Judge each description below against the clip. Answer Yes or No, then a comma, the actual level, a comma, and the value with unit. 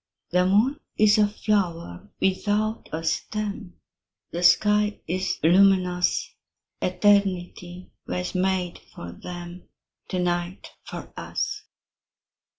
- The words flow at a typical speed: No, slow, 100 wpm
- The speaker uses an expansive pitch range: No, average, 2.7 semitones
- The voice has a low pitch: No, medium, 185 Hz